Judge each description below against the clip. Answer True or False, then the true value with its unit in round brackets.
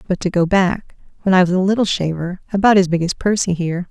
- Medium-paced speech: False (230 wpm)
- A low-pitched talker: False (185 Hz)